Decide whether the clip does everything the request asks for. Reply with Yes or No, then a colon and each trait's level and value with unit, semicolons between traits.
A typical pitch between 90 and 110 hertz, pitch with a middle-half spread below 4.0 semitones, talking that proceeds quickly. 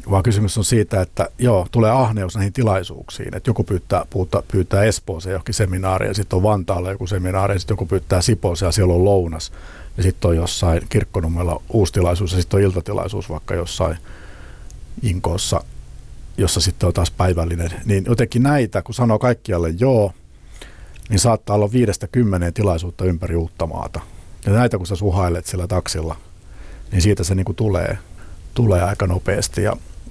Yes: very low, 95 Hz; average, 2.9 semitones; fast, 165 wpm